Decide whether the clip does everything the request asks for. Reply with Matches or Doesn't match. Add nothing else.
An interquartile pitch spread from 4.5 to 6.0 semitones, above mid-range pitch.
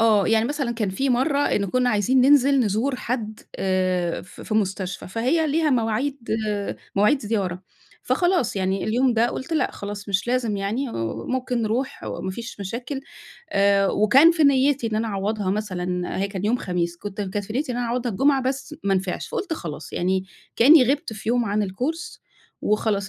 Matches